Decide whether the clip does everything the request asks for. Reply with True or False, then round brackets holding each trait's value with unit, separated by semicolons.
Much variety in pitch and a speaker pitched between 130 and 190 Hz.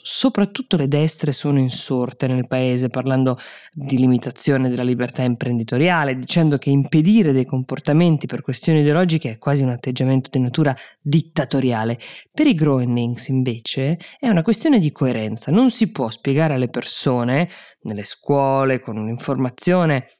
False (3.8 semitones; 135 Hz)